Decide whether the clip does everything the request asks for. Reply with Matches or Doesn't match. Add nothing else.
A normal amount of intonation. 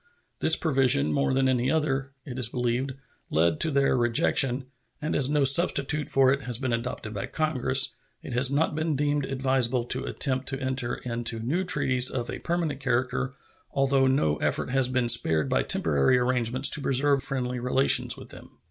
Doesn't match